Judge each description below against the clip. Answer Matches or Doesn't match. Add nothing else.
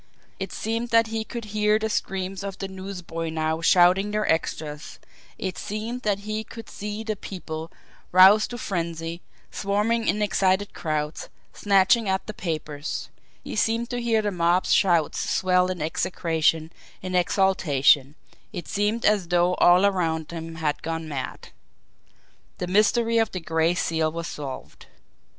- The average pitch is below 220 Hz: Matches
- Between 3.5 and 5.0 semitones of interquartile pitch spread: Matches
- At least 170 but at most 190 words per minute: Doesn't match